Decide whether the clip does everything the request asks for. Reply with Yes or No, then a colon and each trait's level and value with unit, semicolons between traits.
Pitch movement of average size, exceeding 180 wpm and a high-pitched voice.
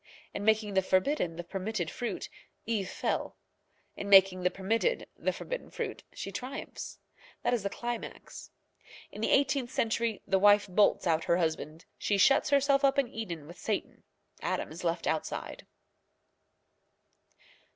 No: average, 4.6 semitones; average, 150 wpm; high, 205 Hz